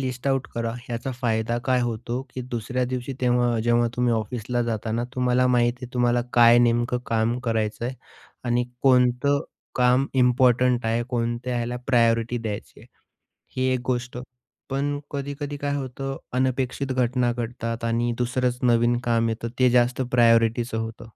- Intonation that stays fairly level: Yes, narrow, 1.4 semitones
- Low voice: Yes, low, 120 Hz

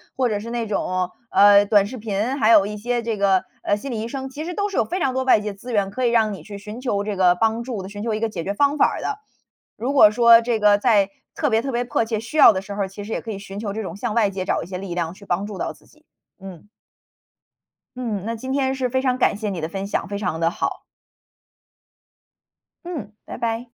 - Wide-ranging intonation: No, average, 3.4 semitones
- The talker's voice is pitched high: Yes, high, 215 Hz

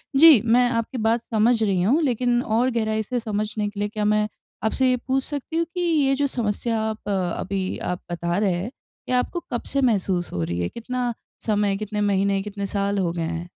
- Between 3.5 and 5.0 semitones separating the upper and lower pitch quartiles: Yes, average, 3.8 semitones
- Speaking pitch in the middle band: No, high, 215 Hz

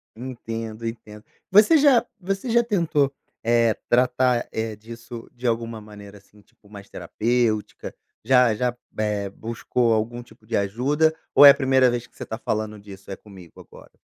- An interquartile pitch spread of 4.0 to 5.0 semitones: No, average, 3.0 semitones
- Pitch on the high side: No, low, 115 Hz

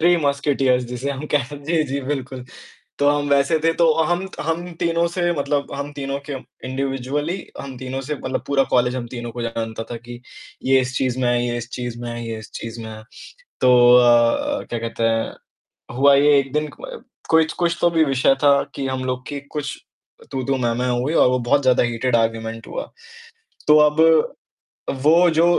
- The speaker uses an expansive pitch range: No, average, 3.2 semitones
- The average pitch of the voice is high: No, low, 135 Hz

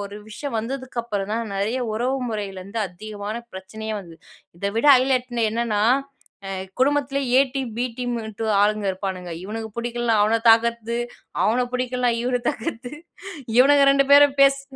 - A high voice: Yes, high, 230 Hz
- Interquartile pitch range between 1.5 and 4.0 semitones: Yes, average, 3.2 semitones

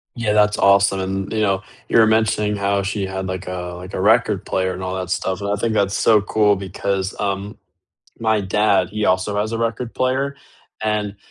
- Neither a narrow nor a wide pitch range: No, narrow, 2.1 semitones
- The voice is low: Yes, low, 100 Hz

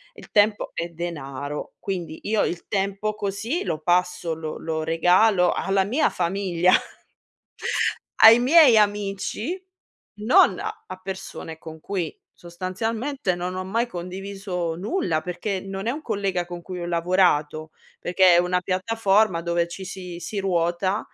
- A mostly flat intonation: No, average, 3.2 semitones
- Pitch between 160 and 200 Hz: Yes, medium, 185 Hz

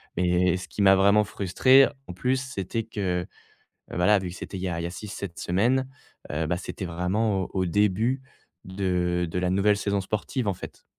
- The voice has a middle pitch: No, very low, 95 Hz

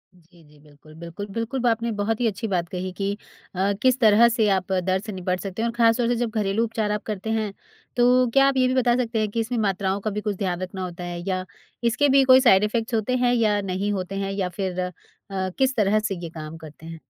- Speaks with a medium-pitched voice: No, high, 205 Hz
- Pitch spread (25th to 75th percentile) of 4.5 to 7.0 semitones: No, average, 3.8 semitones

